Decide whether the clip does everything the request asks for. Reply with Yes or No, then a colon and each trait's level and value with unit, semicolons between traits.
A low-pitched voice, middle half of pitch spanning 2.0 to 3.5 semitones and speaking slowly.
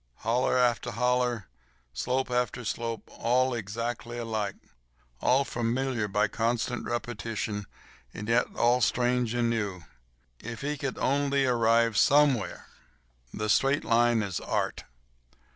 Yes: low, 120 Hz; narrow, 2.4 semitones; slow, 110 wpm